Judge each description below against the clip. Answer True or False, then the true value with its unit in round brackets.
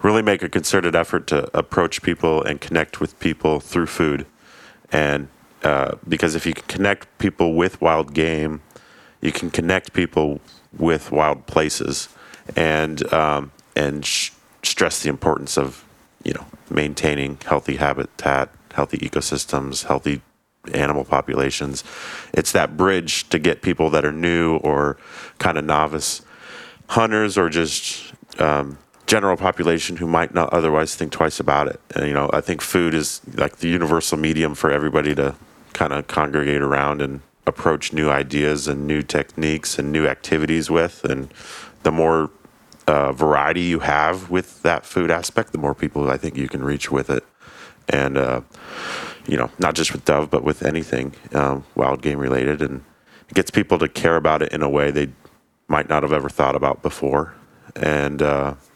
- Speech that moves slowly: False (165 wpm)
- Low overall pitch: True (75 Hz)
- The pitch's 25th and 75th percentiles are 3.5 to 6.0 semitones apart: False (2.6 semitones)